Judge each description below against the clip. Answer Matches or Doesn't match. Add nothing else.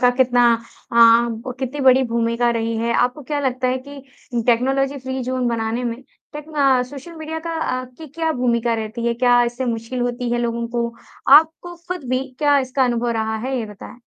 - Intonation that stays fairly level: Matches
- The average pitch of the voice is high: Matches